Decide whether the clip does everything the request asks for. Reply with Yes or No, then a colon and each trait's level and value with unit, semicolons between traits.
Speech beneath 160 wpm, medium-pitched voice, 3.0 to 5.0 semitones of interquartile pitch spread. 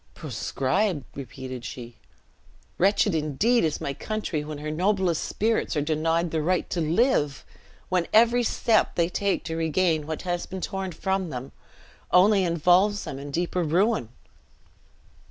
Yes: average, 145 wpm; medium, 170 Hz; average, 4.3 semitones